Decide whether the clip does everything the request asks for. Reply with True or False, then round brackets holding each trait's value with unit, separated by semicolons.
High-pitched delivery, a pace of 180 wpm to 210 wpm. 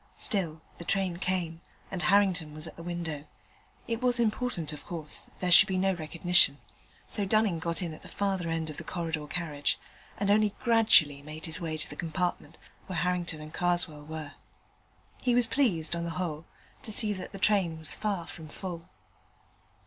False (175 Hz; 185 wpm)